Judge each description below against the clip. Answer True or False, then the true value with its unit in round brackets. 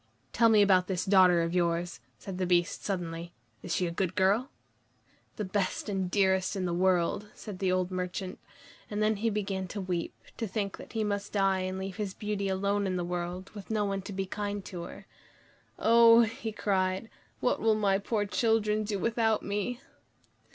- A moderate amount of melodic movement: False (2.3 semitones)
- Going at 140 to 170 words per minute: False (195 wpm)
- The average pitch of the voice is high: True (195 Hz)